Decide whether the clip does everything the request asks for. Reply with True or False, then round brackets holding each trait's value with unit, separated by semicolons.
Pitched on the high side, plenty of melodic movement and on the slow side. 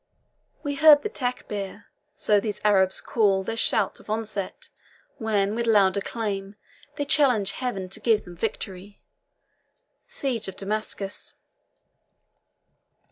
False (210 Hz; 2.9 semitones; 120 wpm)